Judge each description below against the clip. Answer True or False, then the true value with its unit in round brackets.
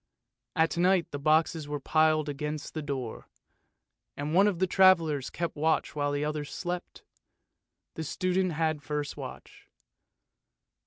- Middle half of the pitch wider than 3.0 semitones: False (2.7 semitones)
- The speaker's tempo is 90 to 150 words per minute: True (145 wpm)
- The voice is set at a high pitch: False (155 Hz)